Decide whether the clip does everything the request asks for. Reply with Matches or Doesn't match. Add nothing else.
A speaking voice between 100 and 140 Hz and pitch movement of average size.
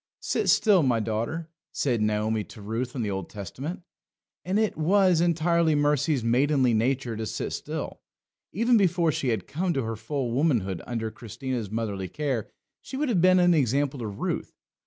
Doesn't match